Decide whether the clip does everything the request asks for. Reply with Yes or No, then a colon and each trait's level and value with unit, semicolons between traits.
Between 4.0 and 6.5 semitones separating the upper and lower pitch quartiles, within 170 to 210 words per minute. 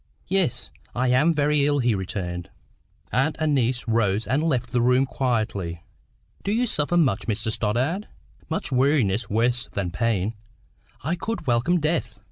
No: wide, 5.4 semitones; average, 150 wpm